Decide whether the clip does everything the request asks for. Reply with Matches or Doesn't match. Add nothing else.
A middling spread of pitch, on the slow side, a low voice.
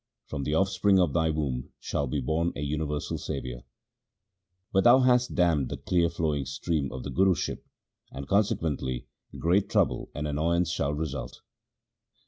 Doesn't match